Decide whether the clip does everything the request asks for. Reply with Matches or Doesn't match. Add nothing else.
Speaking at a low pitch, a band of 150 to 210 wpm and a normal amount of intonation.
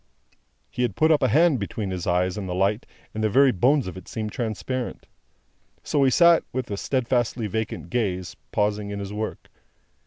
Matches